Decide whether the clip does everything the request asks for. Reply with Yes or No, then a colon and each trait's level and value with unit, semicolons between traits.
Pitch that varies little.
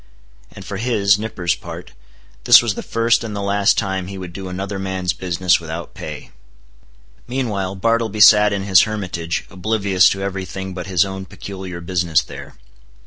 Yes: narrow, 2.0 semitones